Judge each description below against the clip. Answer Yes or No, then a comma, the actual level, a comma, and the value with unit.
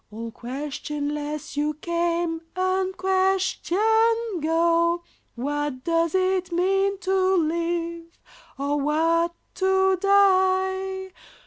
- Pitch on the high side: Yes, very high, 345 Hz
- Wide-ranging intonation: No, average, 3.6 semitones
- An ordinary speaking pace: No, slow, 85 wpm